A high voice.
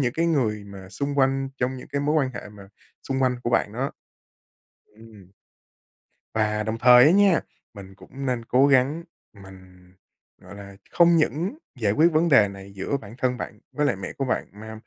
No: low, 125 Hz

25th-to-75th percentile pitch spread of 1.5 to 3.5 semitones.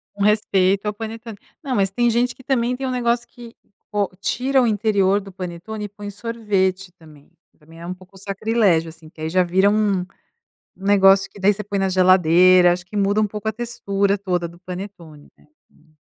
Yes: average, 3.0 semitones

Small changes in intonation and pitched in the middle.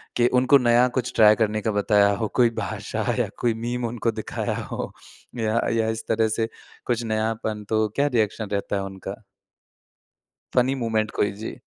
No: narrow, 1.8 semitones; low, 110 Hz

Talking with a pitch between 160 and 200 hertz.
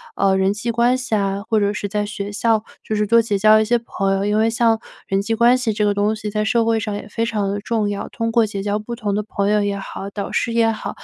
No: high, 215 Hz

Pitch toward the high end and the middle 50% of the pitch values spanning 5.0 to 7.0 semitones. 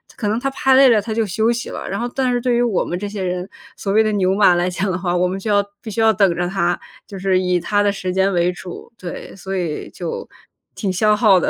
No: high, 195 Hz; average, 3.3 semitones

